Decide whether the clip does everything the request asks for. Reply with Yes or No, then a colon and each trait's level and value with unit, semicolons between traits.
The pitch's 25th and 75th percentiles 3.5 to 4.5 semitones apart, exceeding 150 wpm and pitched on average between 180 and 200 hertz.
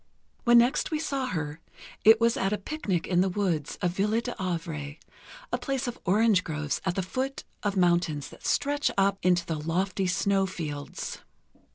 No: average, 5.1 semitones; average, 175 wpm; high, 190 Hz